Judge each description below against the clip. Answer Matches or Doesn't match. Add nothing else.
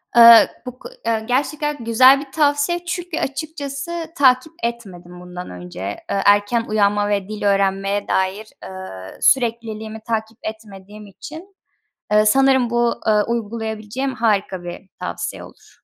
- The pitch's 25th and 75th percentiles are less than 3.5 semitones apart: Doesn't match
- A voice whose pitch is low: Doesn't match